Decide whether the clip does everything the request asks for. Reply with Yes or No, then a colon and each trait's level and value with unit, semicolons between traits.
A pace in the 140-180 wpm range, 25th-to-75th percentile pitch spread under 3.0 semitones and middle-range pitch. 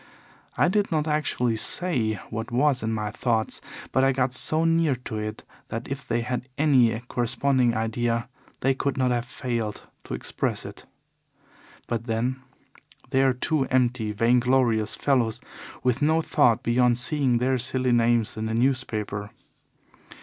No: average, 150 wpm; narrow, 2.6 semitones; low, 125 Hz